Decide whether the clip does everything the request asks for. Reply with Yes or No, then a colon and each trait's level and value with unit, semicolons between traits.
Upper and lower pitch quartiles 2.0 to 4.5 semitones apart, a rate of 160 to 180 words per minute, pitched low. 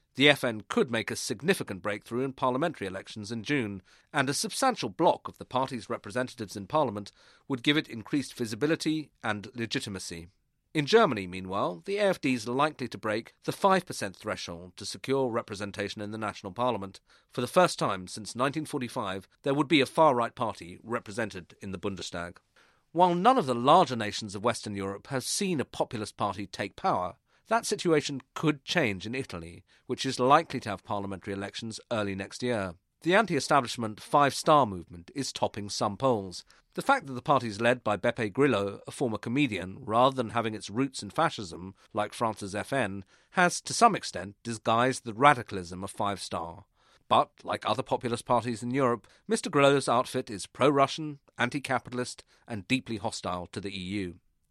No: wide, 5.4 semitones; average, 175 wpm; low, 120 Hz